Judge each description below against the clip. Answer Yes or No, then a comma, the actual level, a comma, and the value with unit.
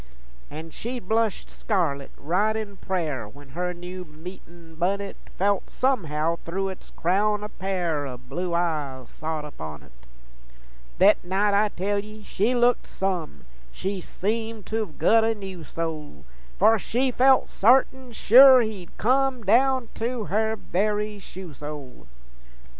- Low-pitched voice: No, high, 190 Hz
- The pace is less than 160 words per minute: Yes, average, 140 wpm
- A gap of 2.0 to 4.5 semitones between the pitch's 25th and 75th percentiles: No, average, 5.2 semitones